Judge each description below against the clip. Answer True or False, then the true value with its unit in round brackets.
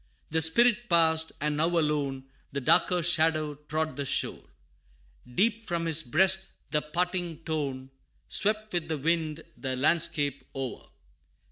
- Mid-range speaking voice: True (160 Hz)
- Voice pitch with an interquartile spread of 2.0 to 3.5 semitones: True (2.8 semitones)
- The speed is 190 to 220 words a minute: False (135 wpm)